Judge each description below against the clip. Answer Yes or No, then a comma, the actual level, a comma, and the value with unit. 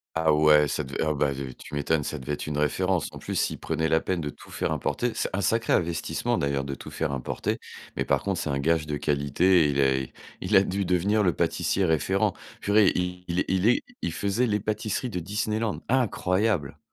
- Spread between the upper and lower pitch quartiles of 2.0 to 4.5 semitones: No, average, 5.3 semitones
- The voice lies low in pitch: Yes, very low, 85 Hz